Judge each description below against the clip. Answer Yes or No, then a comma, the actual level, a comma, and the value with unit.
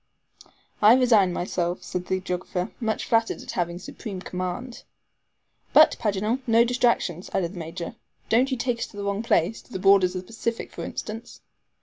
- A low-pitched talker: No, high, 200 Hz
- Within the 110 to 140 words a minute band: No, average, 185 wpm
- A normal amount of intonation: Yes, average, 4.2 semitones